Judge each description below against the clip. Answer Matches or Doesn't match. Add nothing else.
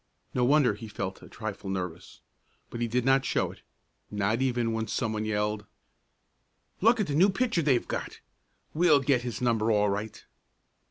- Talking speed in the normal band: Matches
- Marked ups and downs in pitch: Doesn't match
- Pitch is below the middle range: Matches